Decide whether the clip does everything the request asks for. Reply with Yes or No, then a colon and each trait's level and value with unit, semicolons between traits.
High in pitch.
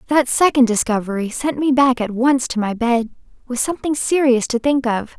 Yes: very high, 250 Hz